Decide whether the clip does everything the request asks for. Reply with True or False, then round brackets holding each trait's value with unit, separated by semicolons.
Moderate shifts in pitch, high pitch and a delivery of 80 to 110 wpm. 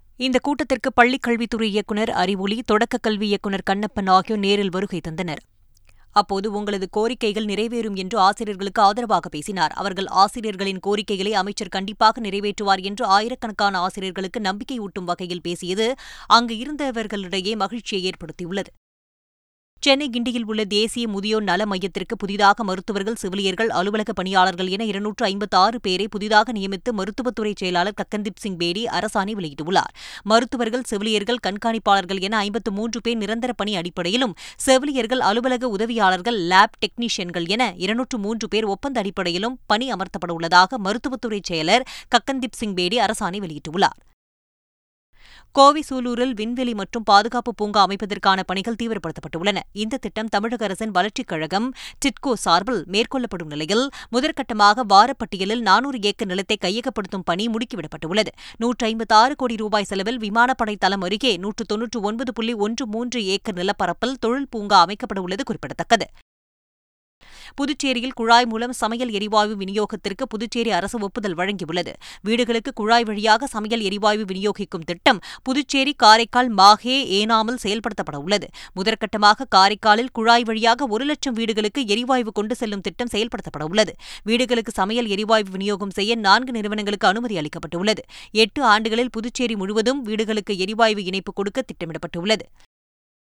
False (3.2 semitones; 215 Hz; 125 wpm)